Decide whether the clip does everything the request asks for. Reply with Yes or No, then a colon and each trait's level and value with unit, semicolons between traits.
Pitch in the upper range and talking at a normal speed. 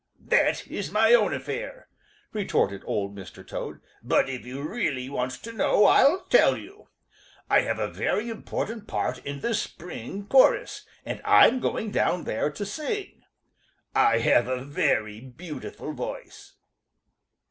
No: medium, 160 Hz; average, 145 wpm